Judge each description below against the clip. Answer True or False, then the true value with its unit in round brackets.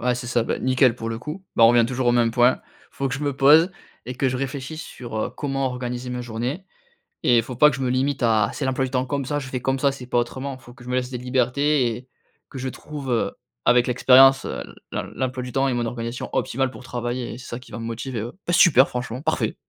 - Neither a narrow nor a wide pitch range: False (1.8 semitones)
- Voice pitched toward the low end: True (125 Hz)